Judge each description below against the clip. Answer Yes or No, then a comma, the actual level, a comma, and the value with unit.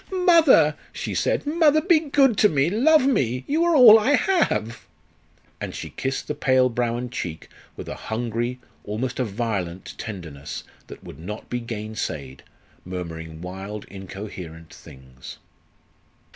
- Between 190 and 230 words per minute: No, average, 145 wpm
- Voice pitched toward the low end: Yes, low, 120 Hz